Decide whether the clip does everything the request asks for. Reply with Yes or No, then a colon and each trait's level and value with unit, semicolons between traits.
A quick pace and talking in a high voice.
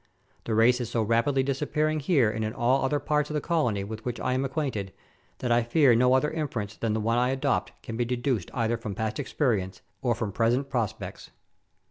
No: fast, 210 wpm; low, 120 Hz